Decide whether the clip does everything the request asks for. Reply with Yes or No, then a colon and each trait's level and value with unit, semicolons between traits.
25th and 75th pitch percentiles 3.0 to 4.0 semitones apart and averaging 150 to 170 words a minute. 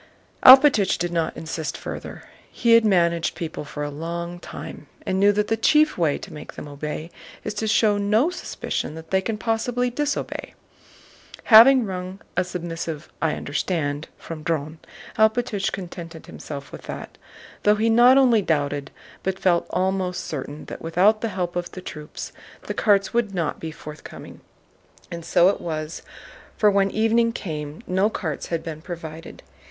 No: average, 5.0 semitones; average, 160 wpm